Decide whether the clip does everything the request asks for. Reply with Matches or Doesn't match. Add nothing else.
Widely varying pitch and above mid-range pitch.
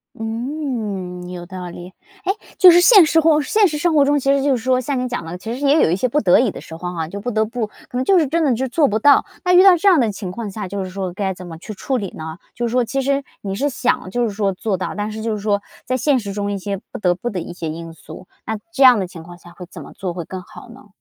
Matches